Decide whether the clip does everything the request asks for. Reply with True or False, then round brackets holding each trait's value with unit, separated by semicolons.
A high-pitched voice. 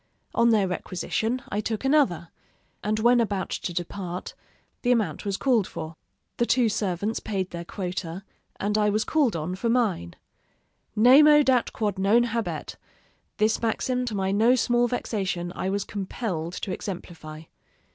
True (210 Hz)